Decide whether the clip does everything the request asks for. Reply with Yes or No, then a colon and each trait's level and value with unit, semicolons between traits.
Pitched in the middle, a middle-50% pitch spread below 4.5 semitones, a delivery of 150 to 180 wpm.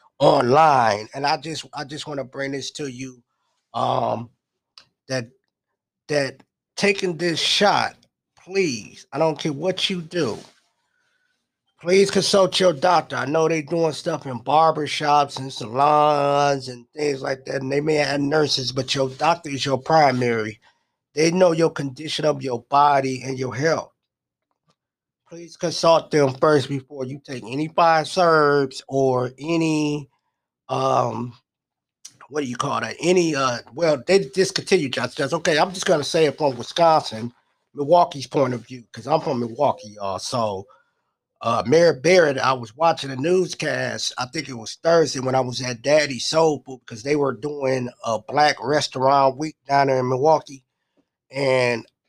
Yes: medium, 145 Hz; average, 3.6 semitones; average, 160 wpm